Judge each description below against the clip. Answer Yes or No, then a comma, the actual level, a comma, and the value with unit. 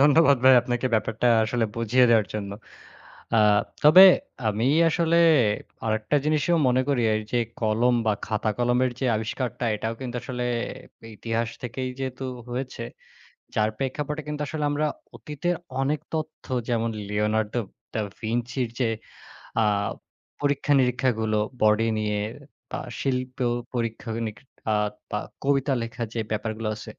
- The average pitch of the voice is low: Yes, low, 120 Hz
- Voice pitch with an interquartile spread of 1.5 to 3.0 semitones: No, average, 3.5 semitones